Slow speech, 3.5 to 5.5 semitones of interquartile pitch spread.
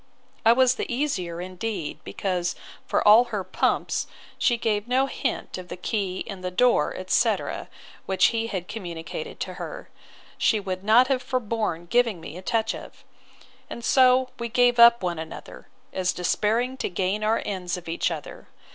No: average, 165 wpm; average, 4.7 semitones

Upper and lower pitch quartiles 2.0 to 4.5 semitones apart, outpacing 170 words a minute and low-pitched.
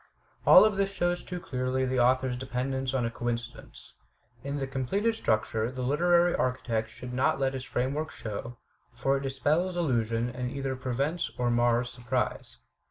No: average, 2.8 semitones; average, 165 wpm; low, 130 Hz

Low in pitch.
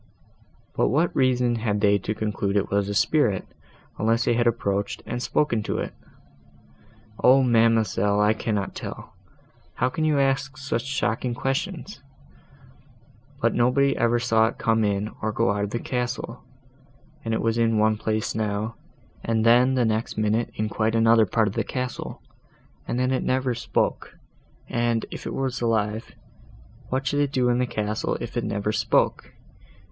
Yes: low, 115 Hz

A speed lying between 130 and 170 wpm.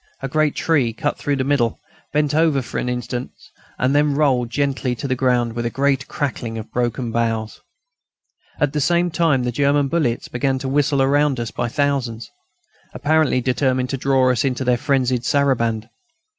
No: average, 180 wpm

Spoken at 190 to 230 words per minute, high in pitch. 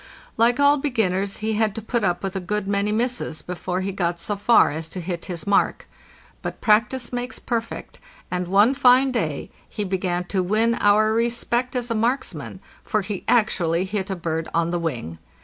Yes: average, 195 wpm; high, 205 Hz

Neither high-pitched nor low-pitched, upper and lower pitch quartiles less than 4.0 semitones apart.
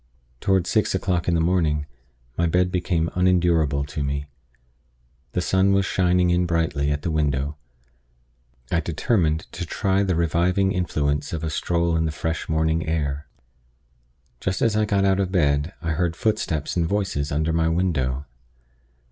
No: very low, 85 Hz; average, 3.0 semitones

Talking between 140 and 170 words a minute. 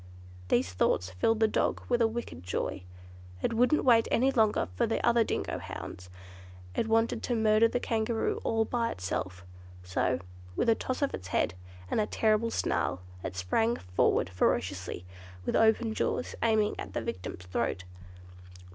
Yes: average, 165 wpm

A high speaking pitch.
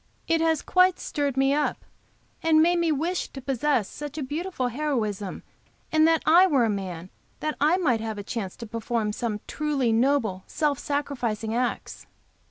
Yes: very high, 275 Hz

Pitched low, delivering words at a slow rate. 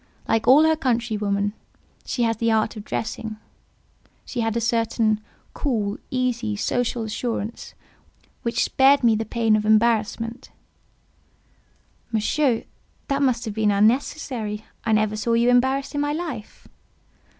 No: high, 230 Hz; slow, 130 wpm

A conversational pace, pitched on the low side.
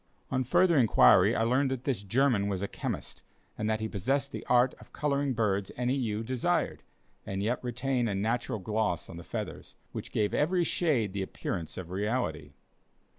Yes: average, 180 wpm; low, 115 Hz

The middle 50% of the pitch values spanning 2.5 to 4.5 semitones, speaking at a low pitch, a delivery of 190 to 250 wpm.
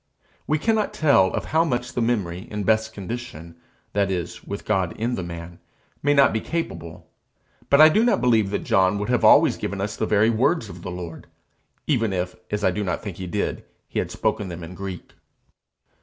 No: average, 4.9 semitones; low, 105 Hz; fast, 205 wpm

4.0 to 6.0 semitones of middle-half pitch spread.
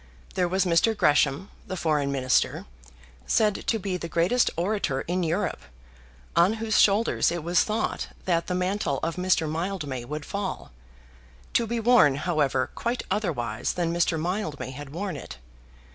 Yes: average, 5.1 semitones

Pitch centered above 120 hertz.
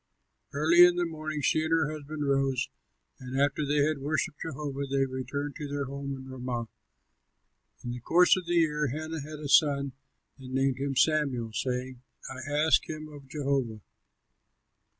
Yes: medium, 140 Hz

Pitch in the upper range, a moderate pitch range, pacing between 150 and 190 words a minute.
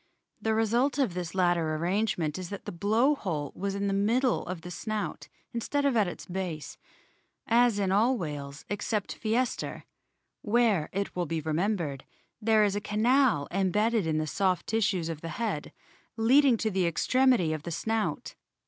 Yes: high, 200 Hz; average, 4.8 semitones; average, 170 wpm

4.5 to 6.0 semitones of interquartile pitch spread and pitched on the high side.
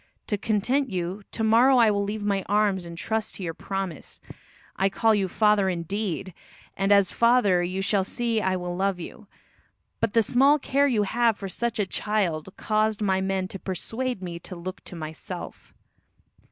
No: average, 3.0 semitones; high, 200 Hz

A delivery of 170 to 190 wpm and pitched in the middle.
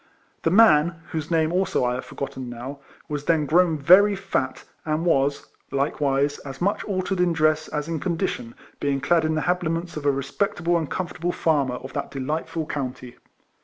Yes: average, 180 wpm; medium, 155 Hz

